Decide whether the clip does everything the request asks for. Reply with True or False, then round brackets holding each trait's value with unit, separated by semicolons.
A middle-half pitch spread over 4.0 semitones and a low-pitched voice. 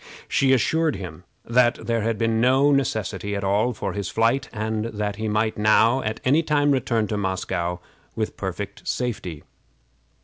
False (3.6 semitones; 110 Hz)